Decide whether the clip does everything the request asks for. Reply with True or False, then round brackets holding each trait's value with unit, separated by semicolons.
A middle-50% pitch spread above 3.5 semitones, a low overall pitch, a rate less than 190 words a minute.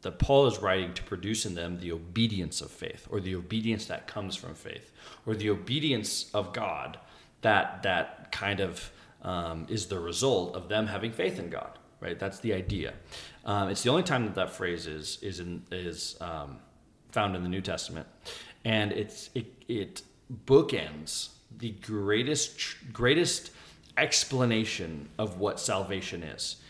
True (4.0 semitones; 100 Hz; 165 wpm)